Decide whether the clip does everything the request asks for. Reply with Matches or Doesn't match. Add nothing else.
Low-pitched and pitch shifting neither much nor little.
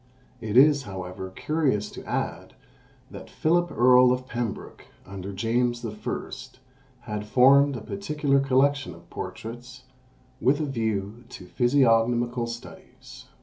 Matches